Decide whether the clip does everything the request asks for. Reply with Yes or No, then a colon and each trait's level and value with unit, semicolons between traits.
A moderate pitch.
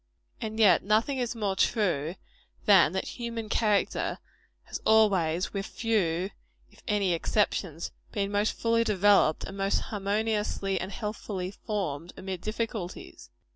No: high, 205 Hz